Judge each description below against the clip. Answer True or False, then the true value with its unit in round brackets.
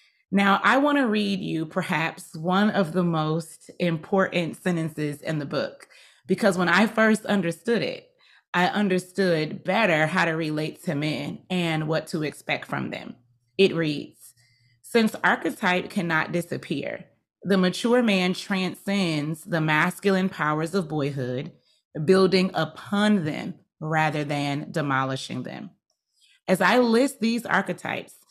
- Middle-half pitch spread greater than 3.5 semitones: True (4.1 semitones)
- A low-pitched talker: False (180 Hz)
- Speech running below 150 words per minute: True (135 wpm)